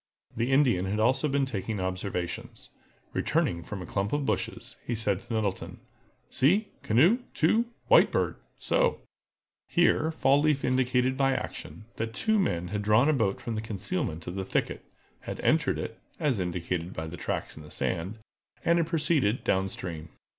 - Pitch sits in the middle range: No, low, 110 Hz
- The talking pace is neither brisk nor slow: Yes, average, 155 wpm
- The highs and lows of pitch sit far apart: Yes, wide, 7.2 semitones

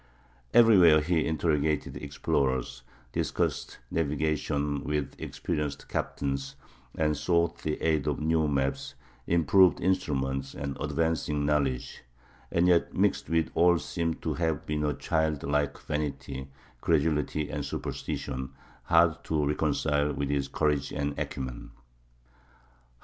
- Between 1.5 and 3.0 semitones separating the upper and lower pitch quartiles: Yes, narrow, 2.4 semitones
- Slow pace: Yes, slow, 115 wpm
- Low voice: Yes, very low, 75 Hz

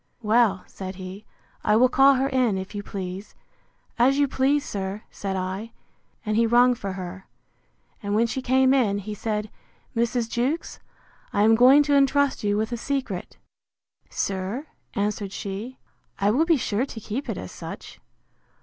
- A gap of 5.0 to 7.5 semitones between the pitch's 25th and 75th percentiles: No, average, 4.6 semitones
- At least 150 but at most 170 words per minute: Yes, average, 165 wpm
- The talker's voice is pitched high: Yes, high, 220 Hz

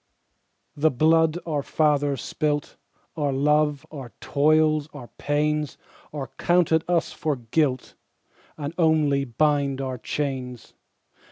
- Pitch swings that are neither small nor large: No, narrow, 2.1 semitones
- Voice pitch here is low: No, medium, 150 Hz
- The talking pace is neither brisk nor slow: No, slow, 110 wpm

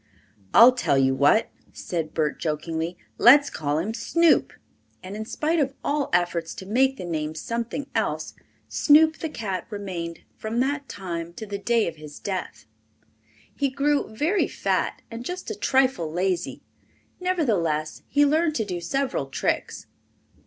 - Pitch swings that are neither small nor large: No, wide, 8.8 semitones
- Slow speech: No, average, 150 wpm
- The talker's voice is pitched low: No, high, 215 Hz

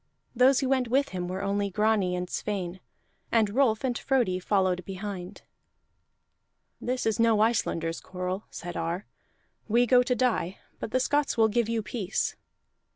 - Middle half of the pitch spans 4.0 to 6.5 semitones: Yes, average, 4.9 semitones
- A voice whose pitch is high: Yes, high, 210 Hz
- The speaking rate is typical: Yes, average, 160 wpm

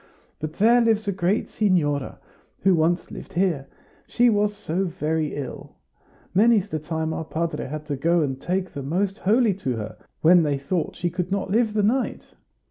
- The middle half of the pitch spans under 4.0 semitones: No, average, 4.8 semitones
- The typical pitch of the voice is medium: Yes, medium, 175 Hz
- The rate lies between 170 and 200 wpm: Yes, average, 185 wpm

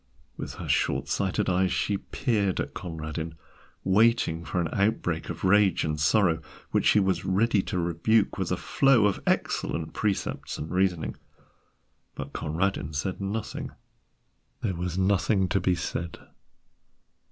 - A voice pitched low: Yes, very low, 95 Hz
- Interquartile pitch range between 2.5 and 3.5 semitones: Yes, average, 3.1 semitones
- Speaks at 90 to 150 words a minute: Yes, average, 140 wpm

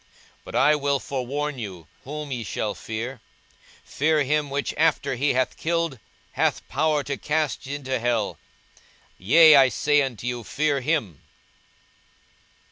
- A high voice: No, medium, 140 Hz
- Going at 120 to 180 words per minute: Yes, average, 140 wpm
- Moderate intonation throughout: Yes, average, 3.4 semitones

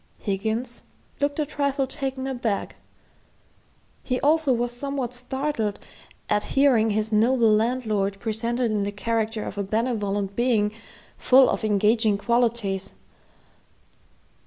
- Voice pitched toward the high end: Yes, high, 230 Hz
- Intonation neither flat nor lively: Yes, average, 3.5 semitones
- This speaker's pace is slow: Yes, slow, 115 wpm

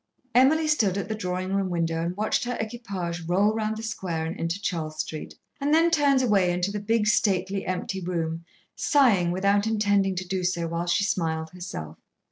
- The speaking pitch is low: No, high, 190 Hz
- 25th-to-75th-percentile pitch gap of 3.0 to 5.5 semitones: Yes, average, 3.9 semitones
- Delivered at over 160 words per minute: Yes, average, 190 wpm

